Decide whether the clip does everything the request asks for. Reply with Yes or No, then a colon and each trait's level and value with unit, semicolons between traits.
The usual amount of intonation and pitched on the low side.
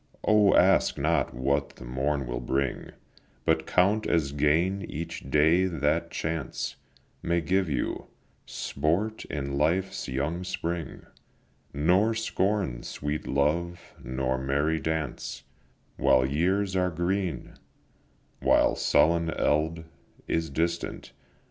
Yes: average, 4.3 semitones; very low, 80 Hz